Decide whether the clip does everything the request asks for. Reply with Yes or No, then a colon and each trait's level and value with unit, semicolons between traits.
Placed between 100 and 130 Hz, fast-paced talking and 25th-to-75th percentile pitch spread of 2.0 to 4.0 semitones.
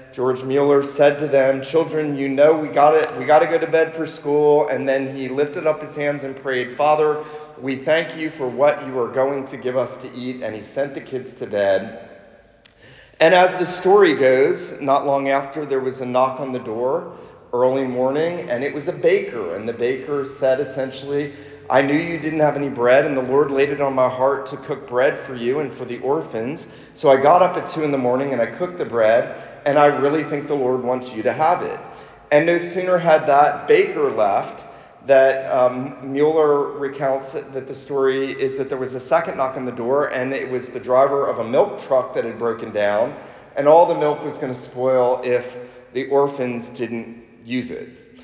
No: medium, 140 Hz; fast, 220 wpm; average, 2.8 semitones